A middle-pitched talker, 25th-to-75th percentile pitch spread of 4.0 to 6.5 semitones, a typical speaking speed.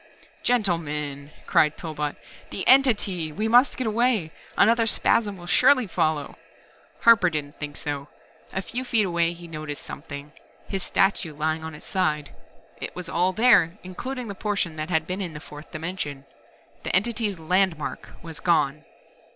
Yes: medium, 175 Hz; average, 5.2 semitones; average, 165 wpm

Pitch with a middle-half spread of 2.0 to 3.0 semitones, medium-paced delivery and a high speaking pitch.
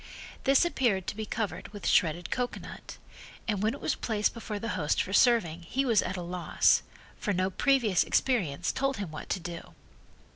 No: average, 5.1 semitones; average, 180 wpm; high, 205 Hz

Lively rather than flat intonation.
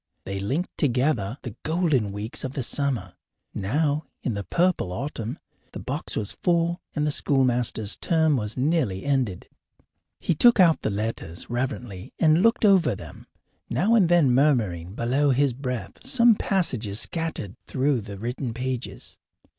Yes: wide, 6.4 semitones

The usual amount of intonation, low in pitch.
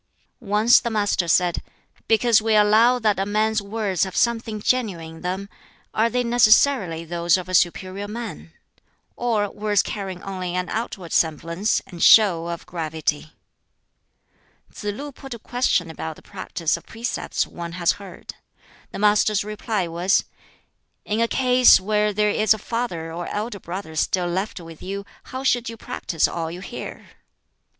No: average, 4.1 semitones; high, 200 Hz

